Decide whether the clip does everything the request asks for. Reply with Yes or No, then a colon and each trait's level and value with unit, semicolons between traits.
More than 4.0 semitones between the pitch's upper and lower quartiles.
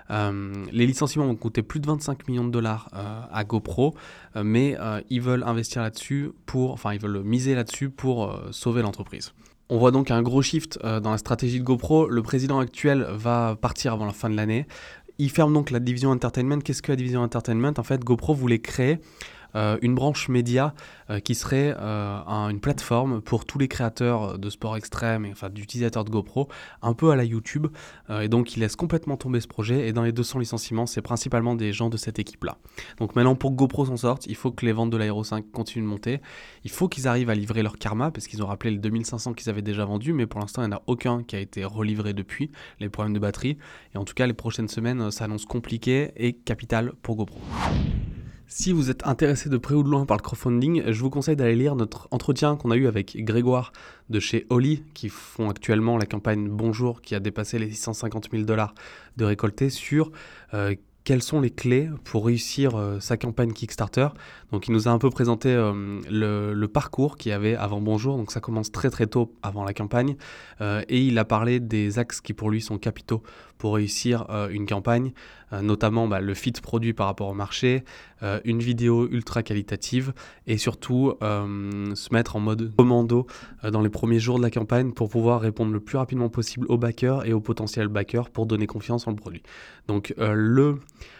No: average, 3.0 semitones